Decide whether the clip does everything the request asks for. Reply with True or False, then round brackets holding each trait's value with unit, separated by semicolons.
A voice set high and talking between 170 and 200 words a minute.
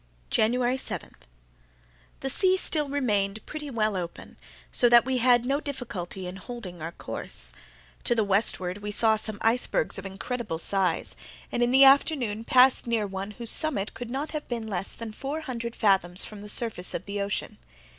True (220 Hz; 180 wpm)